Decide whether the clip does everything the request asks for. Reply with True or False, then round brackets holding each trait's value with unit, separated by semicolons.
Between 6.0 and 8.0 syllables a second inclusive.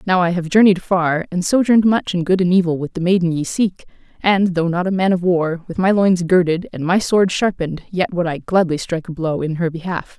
False (5.6 syllables/s)